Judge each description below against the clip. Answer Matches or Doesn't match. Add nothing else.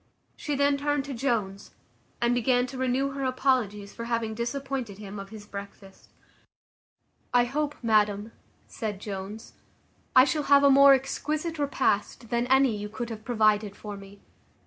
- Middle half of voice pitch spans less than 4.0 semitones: Doesn't match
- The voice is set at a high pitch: Matches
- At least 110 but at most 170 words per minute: Matches